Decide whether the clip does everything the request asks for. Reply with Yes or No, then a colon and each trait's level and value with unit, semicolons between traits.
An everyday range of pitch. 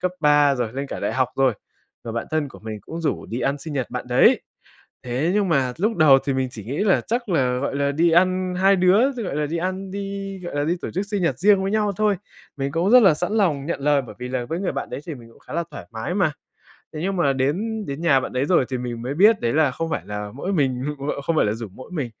No: wide, 6.1 semitones